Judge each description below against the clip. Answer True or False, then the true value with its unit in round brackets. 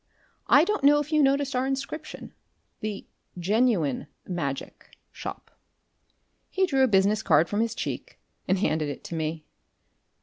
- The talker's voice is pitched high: True (215 Hz)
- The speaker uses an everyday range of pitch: False (8.5 semitones)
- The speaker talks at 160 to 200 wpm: False (145 wpm)